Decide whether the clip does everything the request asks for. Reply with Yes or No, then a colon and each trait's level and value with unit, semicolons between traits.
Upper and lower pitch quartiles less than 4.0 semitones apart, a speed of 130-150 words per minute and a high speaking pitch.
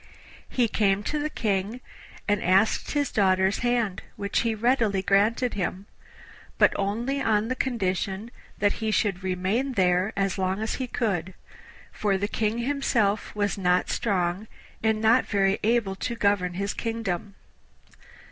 Yes: average, 3.1 semitones; average, 145 wpm; high, 205 Hz